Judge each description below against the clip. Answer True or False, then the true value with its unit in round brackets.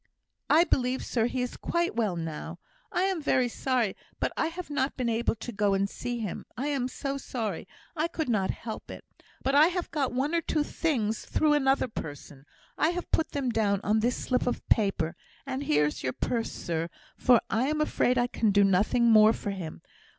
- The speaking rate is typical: False (210 wpm)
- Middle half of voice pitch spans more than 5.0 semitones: True (5.5 semitones)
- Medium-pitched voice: False (245 Hz)